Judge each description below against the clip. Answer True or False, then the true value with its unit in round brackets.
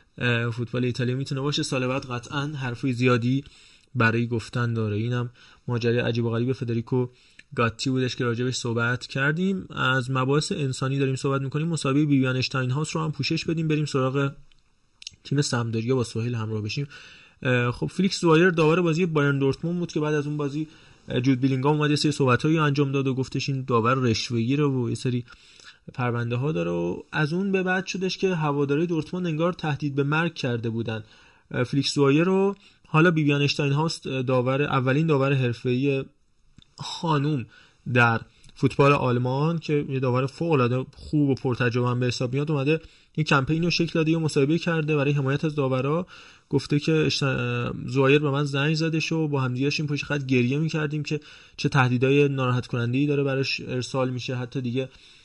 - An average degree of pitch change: True (3.4 semitones)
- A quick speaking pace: True (170 wpm)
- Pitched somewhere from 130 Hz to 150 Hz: True (140 Hz)